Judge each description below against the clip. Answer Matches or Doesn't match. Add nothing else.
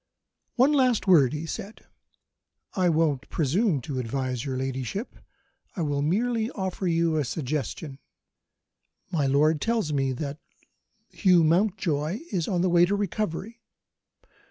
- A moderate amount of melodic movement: Doesn't match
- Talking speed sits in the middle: Doesn't match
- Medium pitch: Matches